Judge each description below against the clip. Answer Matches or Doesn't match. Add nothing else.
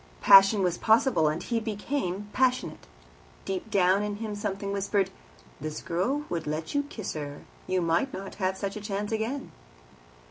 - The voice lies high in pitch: Matches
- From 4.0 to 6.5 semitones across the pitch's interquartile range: Doesn't match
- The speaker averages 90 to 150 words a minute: Doesn't match